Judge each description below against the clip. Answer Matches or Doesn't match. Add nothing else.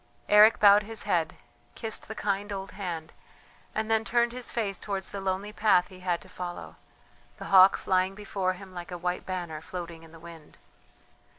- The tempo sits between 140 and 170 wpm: Doesn't match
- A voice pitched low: Doesn't match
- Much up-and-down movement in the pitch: Doesn't match